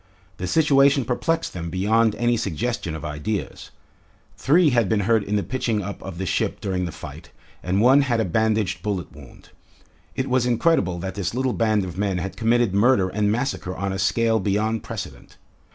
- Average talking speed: Yes, average, 185 wpm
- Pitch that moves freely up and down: No, average, 4.2 semitones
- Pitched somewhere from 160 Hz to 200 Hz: No, low, 105 Hz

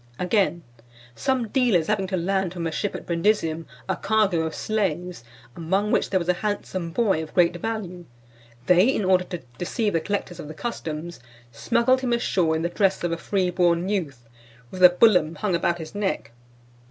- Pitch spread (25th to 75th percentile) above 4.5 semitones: No, average, 3.6 semitones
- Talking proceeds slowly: No, average, 185 wpm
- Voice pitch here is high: No, medium, 180 Hz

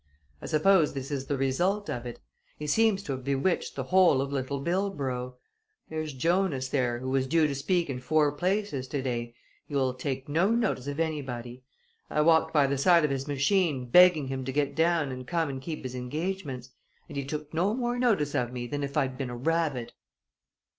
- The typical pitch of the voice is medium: Yes, medium, 145 Hz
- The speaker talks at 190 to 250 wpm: Yes, average, 200 wpm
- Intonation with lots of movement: No, average, 4.3 semitones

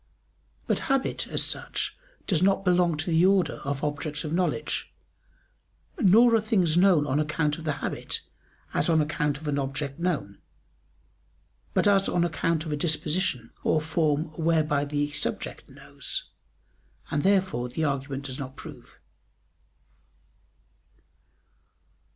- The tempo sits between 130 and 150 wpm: Yes, slow, 135 wpm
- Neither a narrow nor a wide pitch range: Yes, average, 3.4 semitones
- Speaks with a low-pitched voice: No, medium, 155 Hz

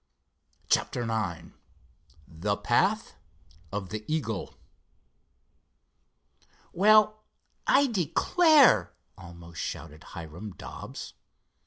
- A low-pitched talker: Yes, low, 110 Hz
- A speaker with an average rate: No, slow, 70 wpm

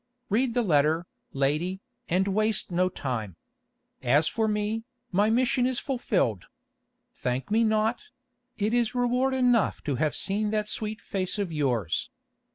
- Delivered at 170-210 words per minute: No, average, 145 wpm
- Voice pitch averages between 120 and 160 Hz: No, high, 210 Hz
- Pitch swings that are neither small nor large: No, wide, 6.7 semitones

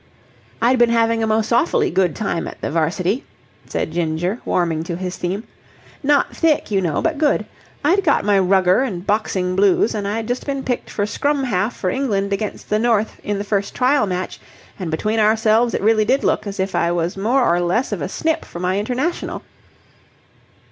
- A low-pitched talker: No, high, 210 Hz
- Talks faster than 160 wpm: Yes, average, 195 wpm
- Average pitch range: Yes, average, 4.8 semitones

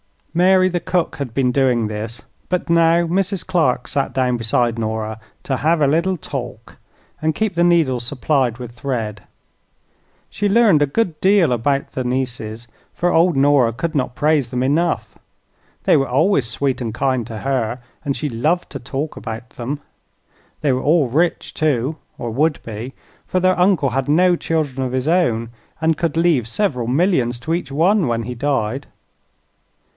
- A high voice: No, medium, 140 Hz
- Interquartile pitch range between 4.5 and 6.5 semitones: Yes, wide, 5.4 semitones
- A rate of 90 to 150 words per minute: No, average, 170 wpm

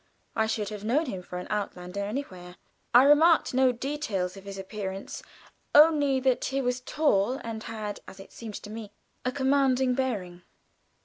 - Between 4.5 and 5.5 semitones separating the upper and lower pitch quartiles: Yes, average, 5.1 semitones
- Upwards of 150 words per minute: Yes, average, 170 wpm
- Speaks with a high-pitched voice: Yes, high, 225 Hz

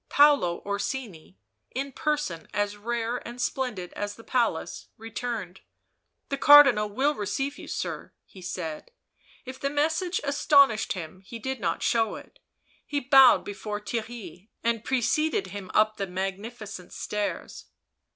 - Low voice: No, high, 225 Hz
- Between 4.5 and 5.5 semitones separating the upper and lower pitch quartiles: Yes, average, 5.0 semitones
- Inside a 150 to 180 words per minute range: No, average, 140 wpm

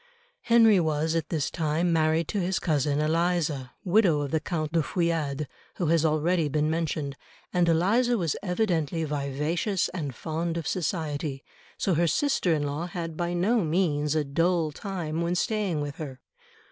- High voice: No, medium, 165 Hz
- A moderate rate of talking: Yes, average, 165 wpm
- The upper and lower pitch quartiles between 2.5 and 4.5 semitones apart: Yes, average, 2.9 semitones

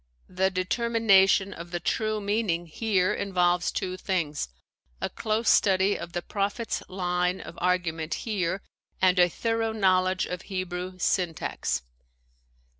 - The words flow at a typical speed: No, slow, 130 wpm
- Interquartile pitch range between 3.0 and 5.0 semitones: No, narrow, 2.4 semitones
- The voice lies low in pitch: No, medium, 185 Hz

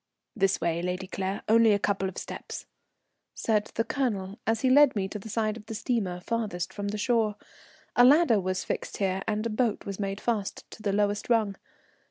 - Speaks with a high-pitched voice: Yes, high, 210 Hz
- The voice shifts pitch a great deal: No, average, 2.8 semitones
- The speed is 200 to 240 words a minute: Yes, fast, 205 wpm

